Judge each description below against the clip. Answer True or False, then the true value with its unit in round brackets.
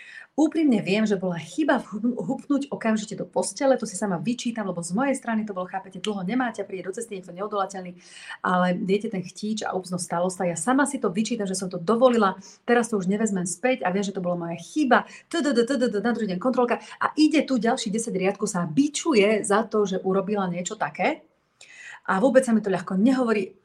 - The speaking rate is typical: False (205 wpm)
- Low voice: False (210 Hz)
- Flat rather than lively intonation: False (4.4 semitones)